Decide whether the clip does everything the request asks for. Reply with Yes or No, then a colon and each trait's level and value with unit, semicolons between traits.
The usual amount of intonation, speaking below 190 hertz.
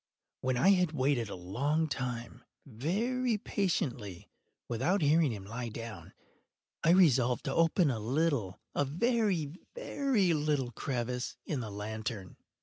No: wide, 6.3 semitones; medium, 140 Hz